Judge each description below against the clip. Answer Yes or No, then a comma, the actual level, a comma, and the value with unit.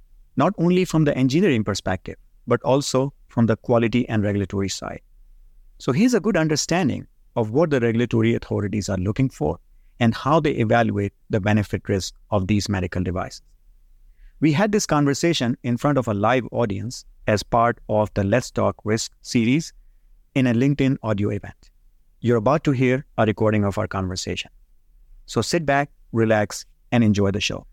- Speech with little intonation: No, average, 4.7 semitones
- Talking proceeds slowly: No, average, 170 wpm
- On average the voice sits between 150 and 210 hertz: No, low, 115 Hz